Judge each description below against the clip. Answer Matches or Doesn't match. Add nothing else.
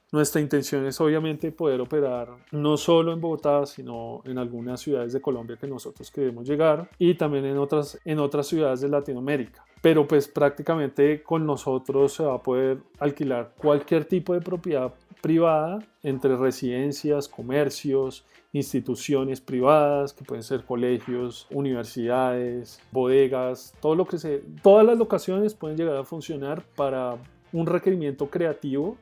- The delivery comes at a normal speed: Matches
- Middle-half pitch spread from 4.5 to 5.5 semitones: Doesn't match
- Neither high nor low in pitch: Matches